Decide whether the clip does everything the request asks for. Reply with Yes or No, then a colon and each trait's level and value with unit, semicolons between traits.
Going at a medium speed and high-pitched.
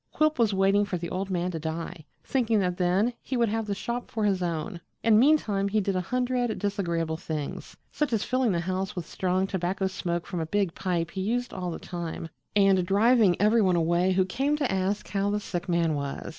No: fast, 220 wpm; high, 195 Hz